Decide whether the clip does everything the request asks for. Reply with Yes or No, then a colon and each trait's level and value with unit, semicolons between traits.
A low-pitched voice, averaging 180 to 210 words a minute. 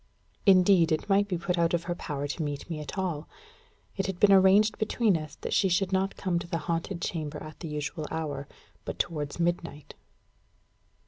No: medium, 170 Hz; average, 195 wpm